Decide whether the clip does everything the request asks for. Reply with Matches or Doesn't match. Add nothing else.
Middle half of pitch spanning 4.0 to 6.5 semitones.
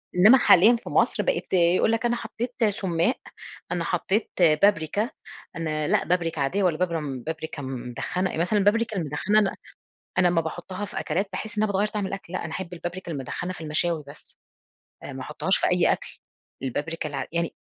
Matches